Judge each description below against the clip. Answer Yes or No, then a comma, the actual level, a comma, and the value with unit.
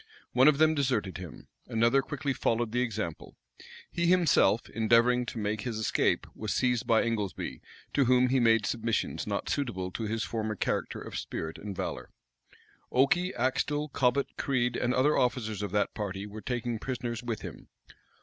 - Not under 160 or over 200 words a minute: Yes, average, 170 wpm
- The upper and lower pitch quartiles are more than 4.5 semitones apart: No, average, 3.2 semitones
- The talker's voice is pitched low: Yes, low, 120 Hz